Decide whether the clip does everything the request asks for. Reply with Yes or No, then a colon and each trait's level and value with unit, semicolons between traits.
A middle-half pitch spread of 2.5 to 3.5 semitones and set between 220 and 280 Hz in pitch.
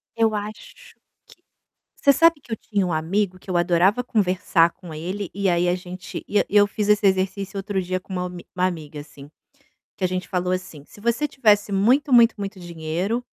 No: average, 2.8 semitones; high, 190 Hz